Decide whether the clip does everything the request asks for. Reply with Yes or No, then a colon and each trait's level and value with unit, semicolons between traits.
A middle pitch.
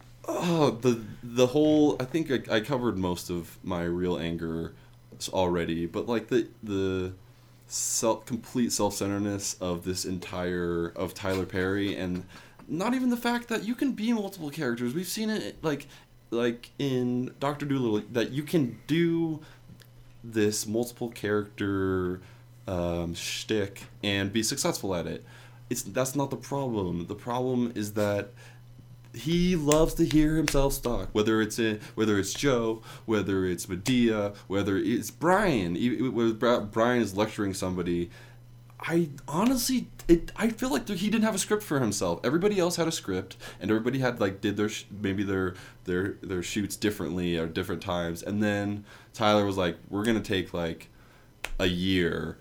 No: low, 115 Hz